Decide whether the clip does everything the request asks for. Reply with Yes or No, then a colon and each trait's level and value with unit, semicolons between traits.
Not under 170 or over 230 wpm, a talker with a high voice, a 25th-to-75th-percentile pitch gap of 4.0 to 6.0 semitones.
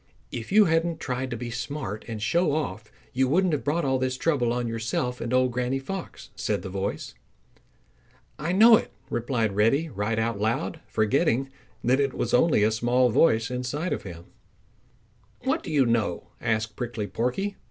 No: average, 175 wpm; low, 125 Hz; average, 4.6 semitones